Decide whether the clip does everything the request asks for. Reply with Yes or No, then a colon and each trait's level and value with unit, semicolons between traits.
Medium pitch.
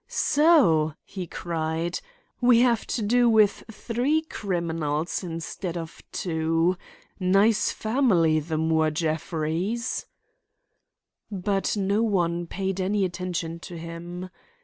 Yes: medium, 180 Hz